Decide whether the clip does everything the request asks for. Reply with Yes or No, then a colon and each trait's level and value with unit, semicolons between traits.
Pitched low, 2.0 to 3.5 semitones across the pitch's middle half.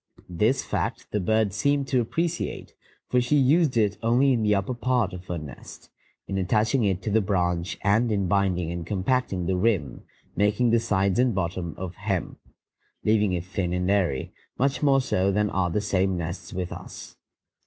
No: low, 100 Hz; average, 4.3 semitones